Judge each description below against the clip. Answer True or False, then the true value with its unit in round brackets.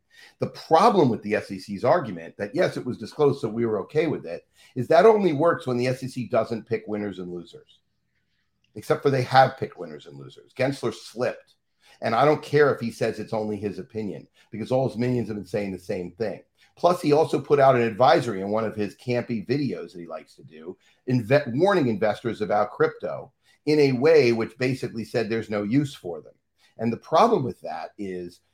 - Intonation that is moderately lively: True (3.6 semitones)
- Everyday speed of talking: False (210 wpm)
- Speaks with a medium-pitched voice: False (115 Hz)